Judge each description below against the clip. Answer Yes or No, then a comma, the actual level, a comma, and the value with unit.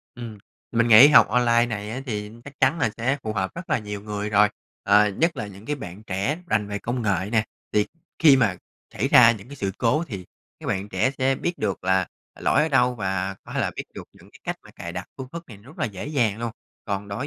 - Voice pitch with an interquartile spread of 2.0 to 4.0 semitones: No, average, 4.4 semitones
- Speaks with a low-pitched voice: Yes, low, 110 Hz